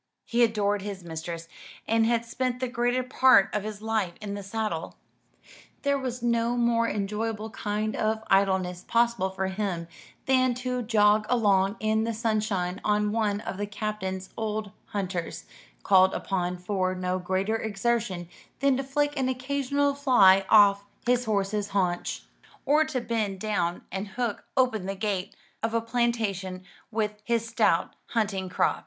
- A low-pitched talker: No, high, 215 Hz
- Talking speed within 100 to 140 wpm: No, average, 155 wpm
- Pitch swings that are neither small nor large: Yes, average, 3.5 semitones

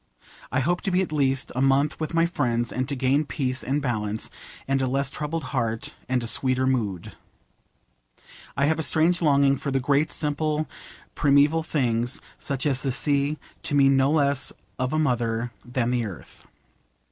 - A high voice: No, low, 135 Hz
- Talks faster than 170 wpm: Yes, average, 180 wpm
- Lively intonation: No, average, 2.9 semitones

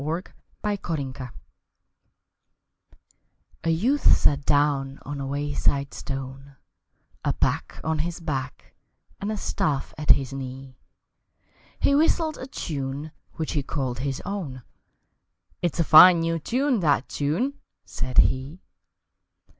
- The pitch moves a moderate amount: Yes, average, 4.3 semitones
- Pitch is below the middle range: No, medium, 145 Hz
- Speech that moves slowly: Yes, slow, 115 wpm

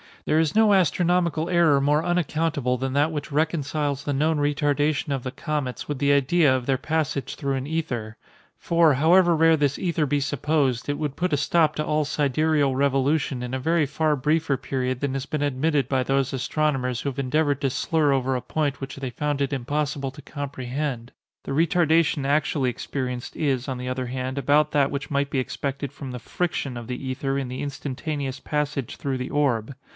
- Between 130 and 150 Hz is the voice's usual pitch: Yes, medium, 140 Hz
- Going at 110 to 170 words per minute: No, average, 195 wpm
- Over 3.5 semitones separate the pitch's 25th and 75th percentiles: No, narrow, 2.6 semitones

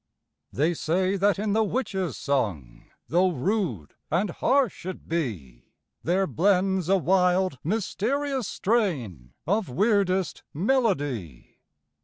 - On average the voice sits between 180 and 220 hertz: Yes, medium, 185 Hz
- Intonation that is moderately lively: No, wide, 6.1 semitones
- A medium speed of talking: No, slow, 110 wpm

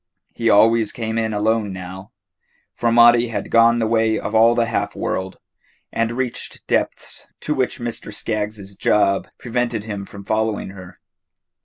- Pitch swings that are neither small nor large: No, narrow, 2.2 semitones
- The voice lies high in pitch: No, low, 110 Hz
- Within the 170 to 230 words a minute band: No, average, 155 wpm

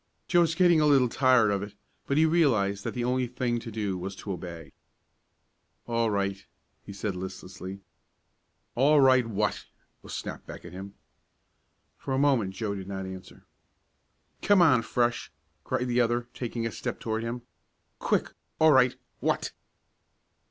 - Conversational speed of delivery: Yes, average, 160 wpm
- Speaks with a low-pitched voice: Yes, low, 115 Hz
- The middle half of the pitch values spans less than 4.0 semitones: No, average, 4.7 semitones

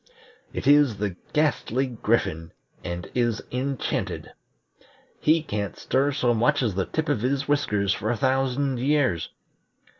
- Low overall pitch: Yes, low, 125 Hz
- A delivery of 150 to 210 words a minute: No, average, 140 wpm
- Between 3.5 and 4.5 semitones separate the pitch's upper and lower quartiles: No, average, 5.3 semitones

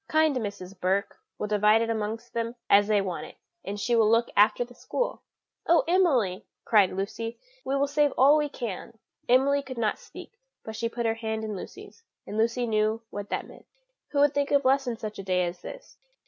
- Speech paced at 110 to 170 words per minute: No, fast, 205 wpm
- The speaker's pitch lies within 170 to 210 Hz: No, high, 230 Hz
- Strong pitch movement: No, average, 4.3 semitones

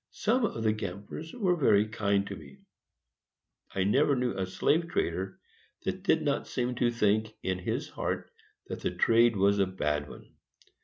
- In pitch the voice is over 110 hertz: No, low, 105 Hz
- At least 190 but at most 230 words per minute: No, average, 170 wpm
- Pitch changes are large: No, average, 4.7 semitones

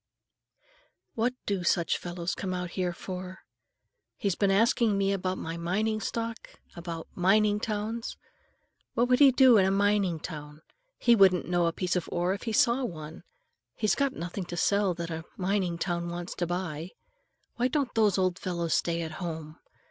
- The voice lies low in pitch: No, medium, 185 Hz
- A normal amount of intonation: Yes, average, 3.6 semitones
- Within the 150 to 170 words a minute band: No, average, 180 wpm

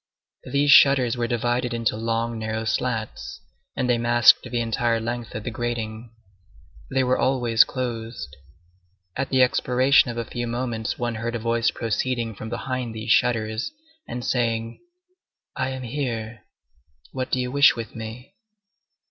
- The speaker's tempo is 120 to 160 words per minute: Yes, average, 150 wpm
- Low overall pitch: Yes, low, 120 Hz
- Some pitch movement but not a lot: No, narrow, 1.8 semitones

